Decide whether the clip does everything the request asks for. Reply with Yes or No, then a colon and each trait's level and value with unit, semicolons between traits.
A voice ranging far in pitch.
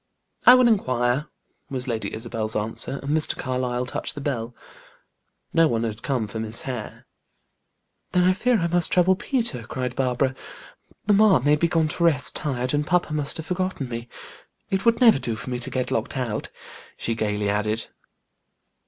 Yes: wide, 6.2 semitones